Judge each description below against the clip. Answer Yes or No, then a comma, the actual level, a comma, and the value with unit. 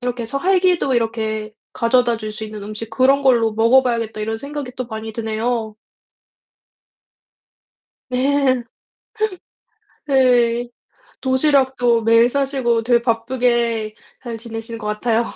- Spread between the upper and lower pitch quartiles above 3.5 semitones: No, narrow, 2.6 semitones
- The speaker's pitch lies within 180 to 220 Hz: No, high, 235 Hz